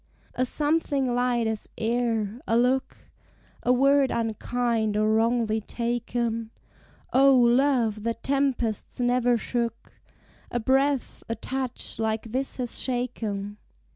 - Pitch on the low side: No, high, 240 Hz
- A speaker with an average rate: No, slow, 115 wpm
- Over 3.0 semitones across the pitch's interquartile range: No, narrow, 2.4 semitones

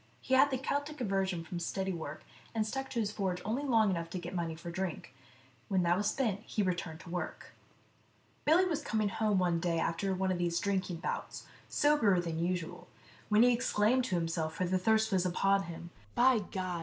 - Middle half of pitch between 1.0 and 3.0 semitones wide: No, average, 4.2 semitones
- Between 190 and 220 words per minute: Yes, fast, 205 wpm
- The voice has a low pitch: No, high, 190 Hz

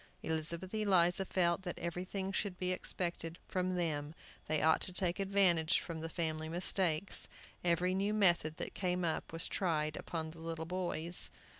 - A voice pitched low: No, medium, 175 Hz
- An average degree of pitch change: No, narrow, 2.3 semitones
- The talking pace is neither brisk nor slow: Yes, average, 160 wpm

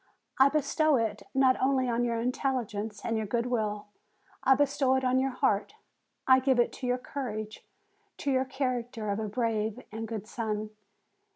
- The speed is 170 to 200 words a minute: Yes, average, 175 wpm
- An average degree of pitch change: Yes, average, 3.3 semitones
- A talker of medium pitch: No, high, 245 Hz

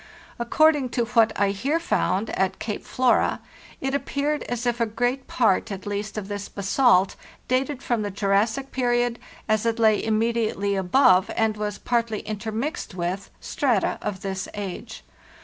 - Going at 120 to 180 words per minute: Yes, average, 160 wpm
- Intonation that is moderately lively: Yes, average, 3.5 semitones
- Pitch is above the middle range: Yes, high, 225 Hz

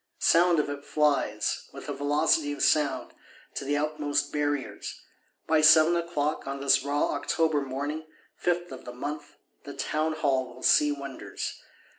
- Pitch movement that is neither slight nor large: No, narrow, 1.9 semitones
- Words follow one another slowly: No, average, 150 wpm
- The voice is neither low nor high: Yes, medium, 145 Hz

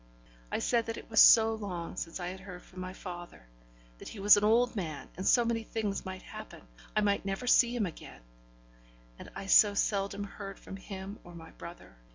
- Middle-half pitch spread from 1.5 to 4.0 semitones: Yes, average, 3.2 semitones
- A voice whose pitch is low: No, high, 195 Hz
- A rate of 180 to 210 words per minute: Yes, fast, 205 wpm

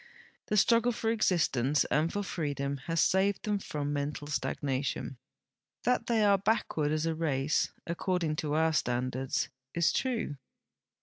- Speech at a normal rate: Yes, average, 145 wpm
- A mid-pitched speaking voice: Yes, medium, 160 Hz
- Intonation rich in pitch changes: Yes, wide, 5.8 semitones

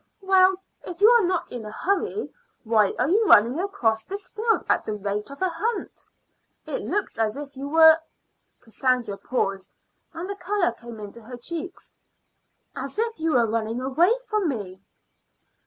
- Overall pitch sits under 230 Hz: No, very high, 285 Hz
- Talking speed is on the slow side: No, average, 170 wpm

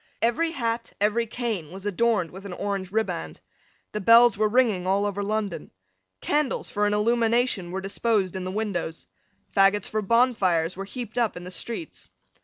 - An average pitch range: Yes, average, 3.5 semitones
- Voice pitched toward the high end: Yes, high, 210 Hz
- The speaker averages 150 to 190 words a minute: Yes, average, 170 wpm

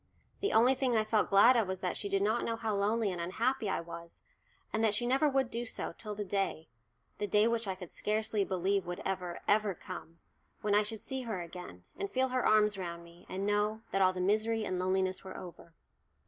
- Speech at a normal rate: No, fast, 230 wpm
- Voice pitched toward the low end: No, high, 205 Hz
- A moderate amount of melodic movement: Yes, average, 3.3 semitones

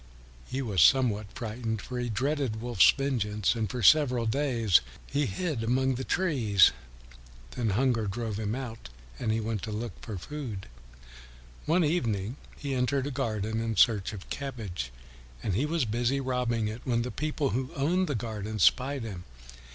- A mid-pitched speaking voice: No, low, 120 Hz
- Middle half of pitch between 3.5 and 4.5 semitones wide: Yes, average, 3.8 semitones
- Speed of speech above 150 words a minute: Yes, average, 170 wpm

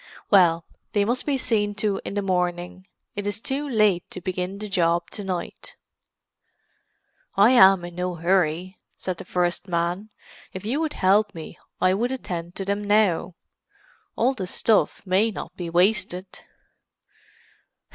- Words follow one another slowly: No, average, 155 wpm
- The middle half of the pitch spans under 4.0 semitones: Yes, average, 2.8 semitones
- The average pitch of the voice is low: No, high, 190 Hz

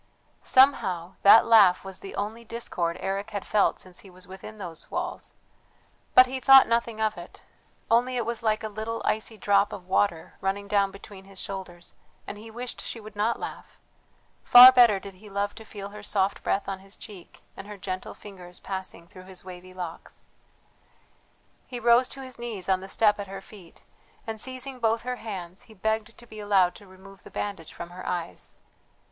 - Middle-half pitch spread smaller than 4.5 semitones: Yes, average, 3.2 semitones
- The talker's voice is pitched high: Yes, high, 205 Hz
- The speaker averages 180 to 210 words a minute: Yes, average, 195 wpm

